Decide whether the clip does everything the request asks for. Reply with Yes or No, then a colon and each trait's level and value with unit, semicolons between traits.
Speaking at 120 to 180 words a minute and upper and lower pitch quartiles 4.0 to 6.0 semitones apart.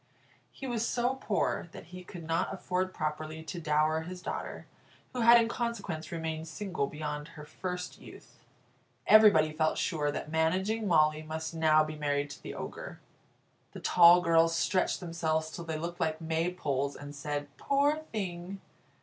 No: average, 160 wpm; average, 3.0 semitones